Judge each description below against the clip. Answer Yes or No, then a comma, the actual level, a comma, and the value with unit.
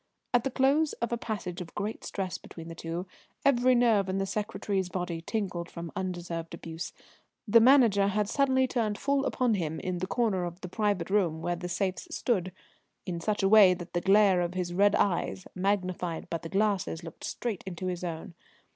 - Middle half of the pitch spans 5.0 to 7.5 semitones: No, average, 3.6 semitones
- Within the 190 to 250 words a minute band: Yes, average, 195 wpm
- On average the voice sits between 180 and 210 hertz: Yes, high, 190 Hz